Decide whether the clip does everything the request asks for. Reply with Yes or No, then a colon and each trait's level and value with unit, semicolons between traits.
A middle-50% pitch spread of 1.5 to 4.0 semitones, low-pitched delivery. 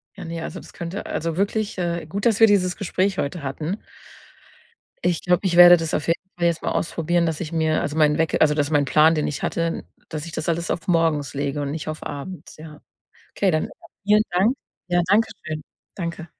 No: narrow, 2.4 semitones; medium, 165 Hz